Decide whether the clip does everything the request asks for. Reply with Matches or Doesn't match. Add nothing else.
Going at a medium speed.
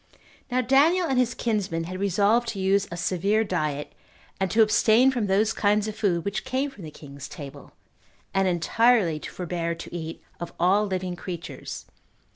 Matches